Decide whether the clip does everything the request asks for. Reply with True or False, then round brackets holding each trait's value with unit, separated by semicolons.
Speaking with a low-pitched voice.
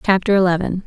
False (185 Hz)